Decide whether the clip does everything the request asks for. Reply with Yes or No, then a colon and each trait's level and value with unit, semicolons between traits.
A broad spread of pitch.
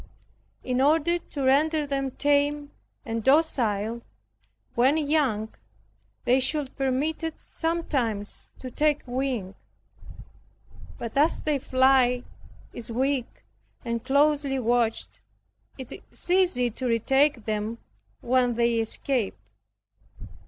No: average, 3.7 semitones